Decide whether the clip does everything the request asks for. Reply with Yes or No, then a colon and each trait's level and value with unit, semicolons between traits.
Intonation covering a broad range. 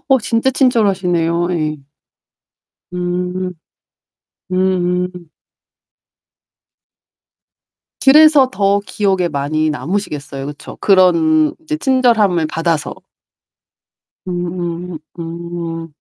No: average, 3.4 semitones